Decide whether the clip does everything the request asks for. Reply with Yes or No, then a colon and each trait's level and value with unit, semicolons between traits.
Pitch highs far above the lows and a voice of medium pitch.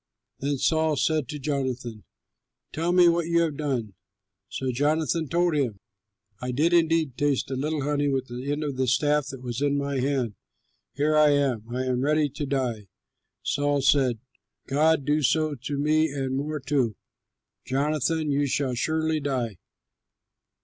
No: average, 2.8 semitones; medium, 145 Hz